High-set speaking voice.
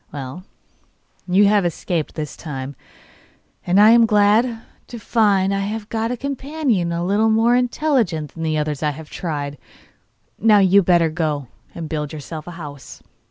No: medium, 180 Hz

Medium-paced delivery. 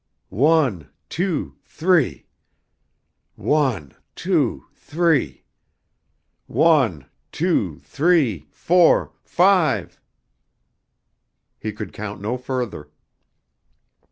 No: slow, 70 wpm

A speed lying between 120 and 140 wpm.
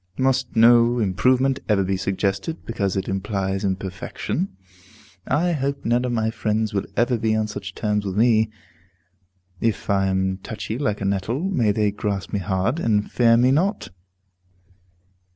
No: average, 155 wpm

